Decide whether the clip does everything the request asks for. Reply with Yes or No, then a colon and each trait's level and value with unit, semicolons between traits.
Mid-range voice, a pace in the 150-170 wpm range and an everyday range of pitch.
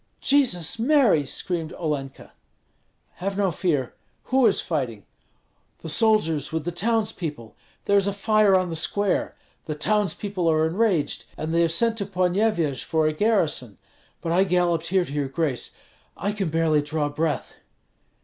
Yes: medium, 170 Hz; average, 155 wpm; average, 4.6 semitones